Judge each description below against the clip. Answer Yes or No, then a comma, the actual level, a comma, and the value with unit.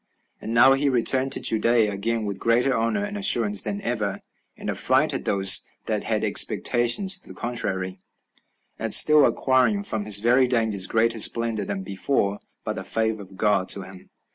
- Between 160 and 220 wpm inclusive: Yes, average, 170 wpm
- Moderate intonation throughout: Yes, average, 4.2 semitones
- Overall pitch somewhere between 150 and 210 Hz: No, low, 115 Hz